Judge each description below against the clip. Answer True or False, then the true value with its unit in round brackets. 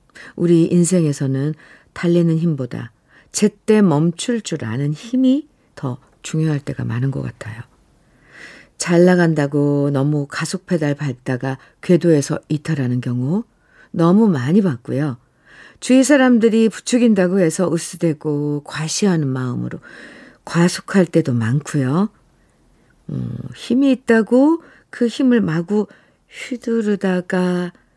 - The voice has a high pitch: False (170 Hz)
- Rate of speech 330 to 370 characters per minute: False (245 characters per minute)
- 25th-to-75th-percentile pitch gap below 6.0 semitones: False (6.3 semitones)